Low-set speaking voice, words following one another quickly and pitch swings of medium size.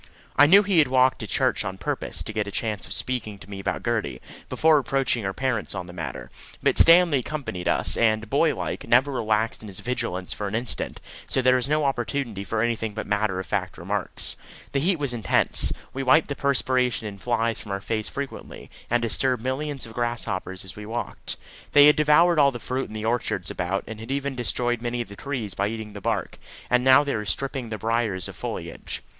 Yes: low, 120 Hz; fast, 215 wpm; average, 4.2 semitones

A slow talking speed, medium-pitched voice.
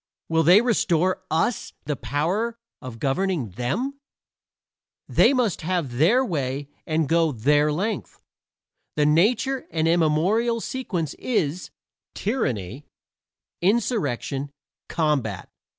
Yes: slow, 105 wpm; medium, 165 Hz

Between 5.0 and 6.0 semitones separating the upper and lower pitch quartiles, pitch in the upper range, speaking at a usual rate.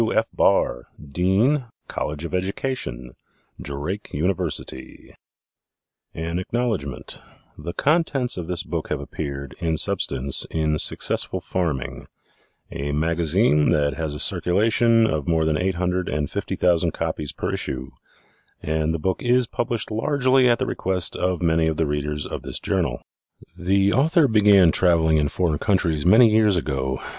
No: wide, 5.6 semitones; very low, 85 Hz; average, 150 wpm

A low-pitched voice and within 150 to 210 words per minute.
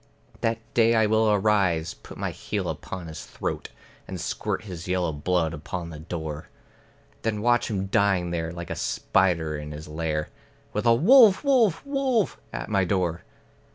Yes: very low, 95 Hz; average, 165 wpm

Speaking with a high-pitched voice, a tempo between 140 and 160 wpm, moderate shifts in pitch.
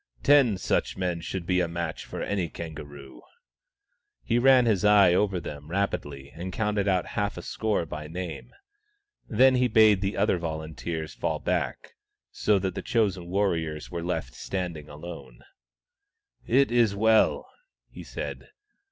No: very low, 90 Hz; average, 150 wpm; average, 4.4 semitones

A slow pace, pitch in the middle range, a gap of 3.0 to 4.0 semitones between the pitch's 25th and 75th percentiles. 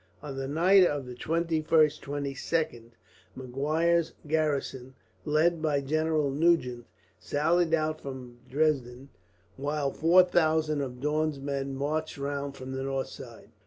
No: slow, 125 wpm; medium, 145 Hz; narrow, 2.6 semitones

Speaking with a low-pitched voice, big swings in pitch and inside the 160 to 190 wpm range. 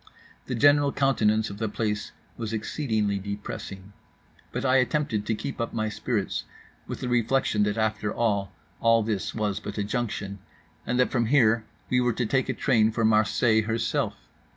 No: low, 110 Hz; average, 2.7 semitones; average, 175 wpm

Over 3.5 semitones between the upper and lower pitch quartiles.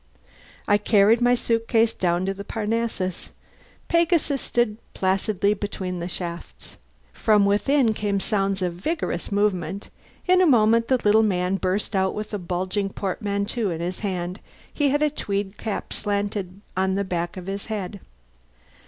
No: average, 3.0 semitones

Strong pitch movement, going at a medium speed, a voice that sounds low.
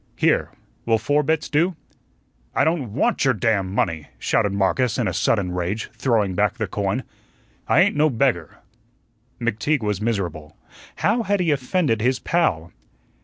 Yes: wide, 7.2 semitones; average, 155 wpm; low, 115 Hz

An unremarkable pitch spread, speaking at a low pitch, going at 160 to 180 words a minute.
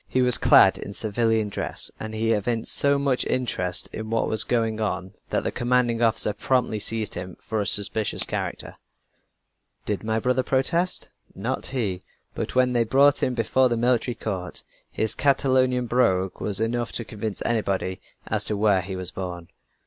Yes: average, 3.6 semitones; low, 115 Hz; average, 170 wpm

